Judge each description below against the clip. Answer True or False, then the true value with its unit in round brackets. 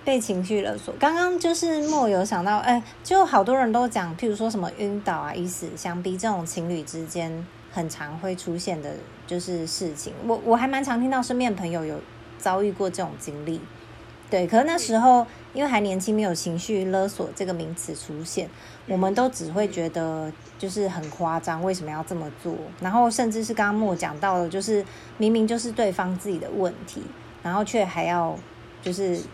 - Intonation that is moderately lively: True (4.8 semitones)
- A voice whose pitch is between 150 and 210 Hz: True (190 Hz)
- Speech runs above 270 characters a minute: True (285 characters per minute)